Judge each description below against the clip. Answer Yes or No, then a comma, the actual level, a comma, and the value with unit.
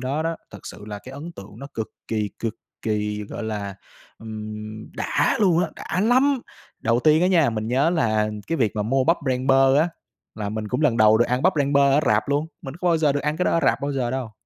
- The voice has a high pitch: No, low, 130 Hz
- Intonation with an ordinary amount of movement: No, wide, 6.0 semitones